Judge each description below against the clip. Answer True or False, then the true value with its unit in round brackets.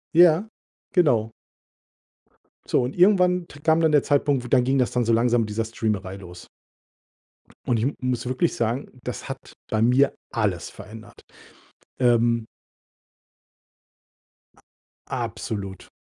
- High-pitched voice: False (120 Hz)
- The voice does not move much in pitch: False (4.5 semitones)